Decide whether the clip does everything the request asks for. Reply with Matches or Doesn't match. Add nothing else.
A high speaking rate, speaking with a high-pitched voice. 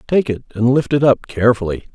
Doesn't match